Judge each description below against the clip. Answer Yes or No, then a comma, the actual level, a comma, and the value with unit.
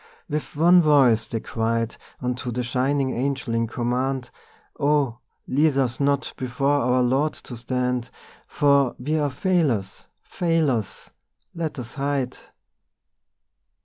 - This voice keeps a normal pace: No, slow, 120 wpm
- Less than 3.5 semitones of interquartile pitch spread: Yes, average, 2.9 semitones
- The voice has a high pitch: No, low, 130 Hz